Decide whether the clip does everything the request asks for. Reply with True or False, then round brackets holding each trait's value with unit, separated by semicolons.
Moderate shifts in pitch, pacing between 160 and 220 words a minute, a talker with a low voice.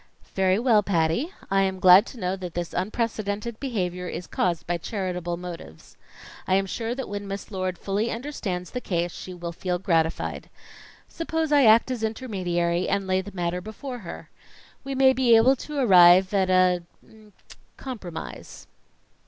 False (4.2 semitones; 165 wpm; 195 Hz)